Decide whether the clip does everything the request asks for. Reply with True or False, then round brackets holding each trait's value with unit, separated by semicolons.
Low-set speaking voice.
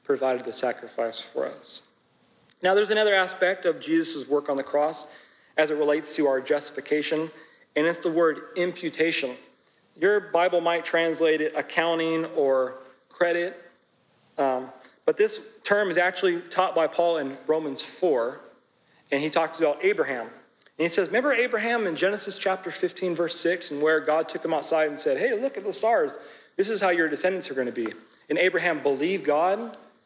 False (170 Hz)